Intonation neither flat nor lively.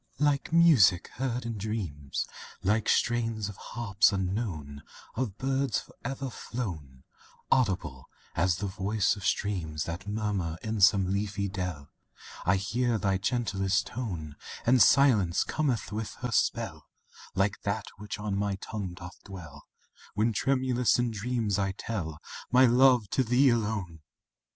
Yes: average, 4.2 semitones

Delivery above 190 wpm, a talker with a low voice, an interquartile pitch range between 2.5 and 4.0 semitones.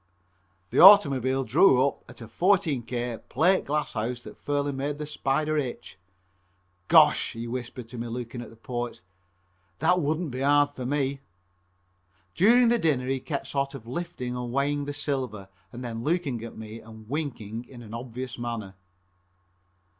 No: average, 160 wpm; low, 130 Hz; average, 3.5 semitones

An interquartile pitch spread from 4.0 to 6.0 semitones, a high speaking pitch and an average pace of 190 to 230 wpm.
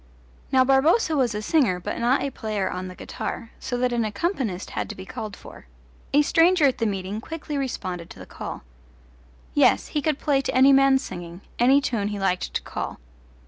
Yes: wide, 5.5 semitones; high, 245 Hz; average, 200 wpm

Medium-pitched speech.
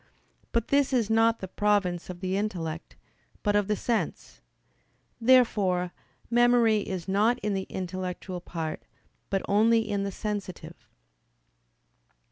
No: high, 205 Hz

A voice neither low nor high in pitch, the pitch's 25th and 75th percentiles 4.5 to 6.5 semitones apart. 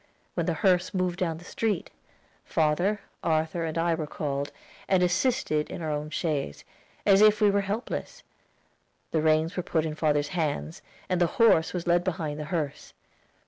No: medium, 165 Hz; average, 3.1 semitones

